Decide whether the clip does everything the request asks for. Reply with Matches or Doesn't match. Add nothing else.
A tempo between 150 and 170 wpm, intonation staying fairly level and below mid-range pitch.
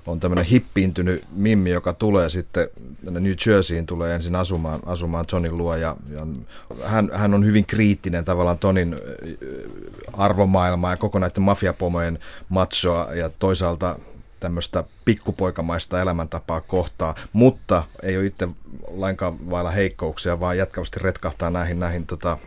Doesn't match